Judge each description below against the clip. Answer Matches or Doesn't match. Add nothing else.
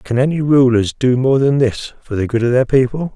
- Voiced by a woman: Doesn't match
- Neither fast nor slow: Doesn't match